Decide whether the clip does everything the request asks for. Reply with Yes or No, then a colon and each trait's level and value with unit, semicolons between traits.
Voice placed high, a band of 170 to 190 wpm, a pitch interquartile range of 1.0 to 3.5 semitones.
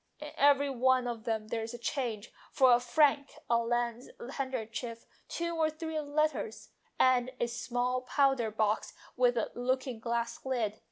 No: high, 245 Hz; average, 160 wpm; average, 2.8 semitones